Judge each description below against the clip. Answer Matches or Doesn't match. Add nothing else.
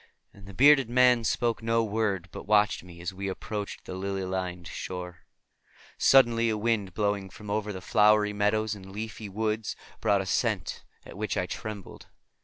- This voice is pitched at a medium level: Doesn't match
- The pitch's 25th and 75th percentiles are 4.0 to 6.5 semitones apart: Doesn't match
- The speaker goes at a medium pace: Matches